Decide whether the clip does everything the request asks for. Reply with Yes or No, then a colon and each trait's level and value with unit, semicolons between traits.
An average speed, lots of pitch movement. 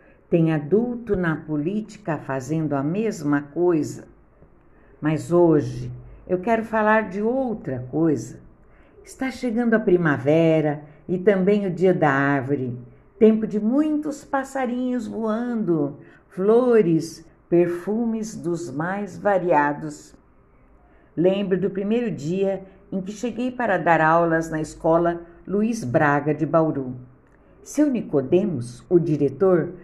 No: slow, 115 wpm; wide, 5.9 semitones